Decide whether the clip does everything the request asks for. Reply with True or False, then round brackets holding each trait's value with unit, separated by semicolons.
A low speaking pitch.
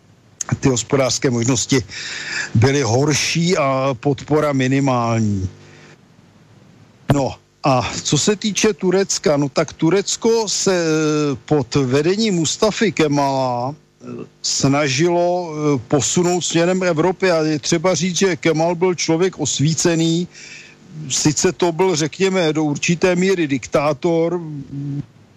False (155 Hz)